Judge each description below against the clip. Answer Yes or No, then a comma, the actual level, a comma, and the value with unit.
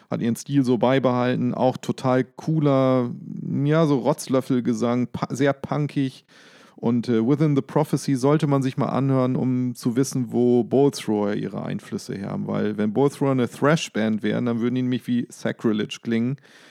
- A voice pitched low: Yes, low, 130 Hz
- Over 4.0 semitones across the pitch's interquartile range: No, average, 2.7 semitones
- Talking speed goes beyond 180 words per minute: No, average, 165 wpm